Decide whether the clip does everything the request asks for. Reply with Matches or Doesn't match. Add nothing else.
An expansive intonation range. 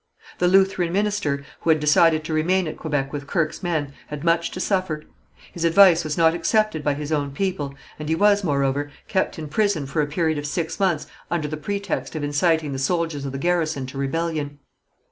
Doesn't match